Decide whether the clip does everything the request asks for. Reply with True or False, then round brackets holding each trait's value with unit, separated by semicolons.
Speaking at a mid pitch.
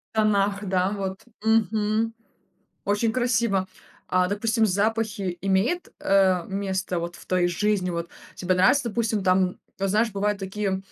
False (200 Hz)